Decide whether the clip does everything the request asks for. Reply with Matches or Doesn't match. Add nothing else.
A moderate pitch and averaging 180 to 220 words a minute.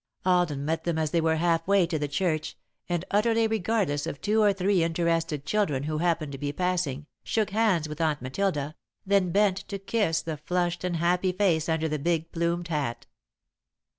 Matches